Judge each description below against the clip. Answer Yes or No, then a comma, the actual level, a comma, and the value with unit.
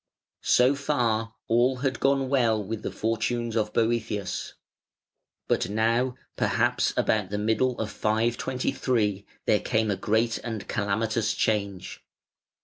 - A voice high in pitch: No, low, 115 Hz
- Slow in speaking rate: Yes, slow, 130 wpm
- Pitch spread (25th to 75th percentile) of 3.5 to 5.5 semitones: No, narrow, 2.4 semitones